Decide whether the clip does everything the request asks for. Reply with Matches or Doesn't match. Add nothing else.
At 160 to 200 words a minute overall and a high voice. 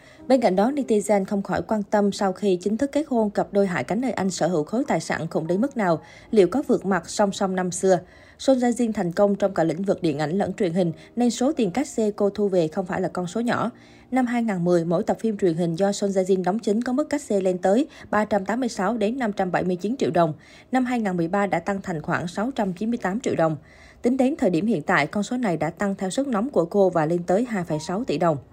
Doesn't match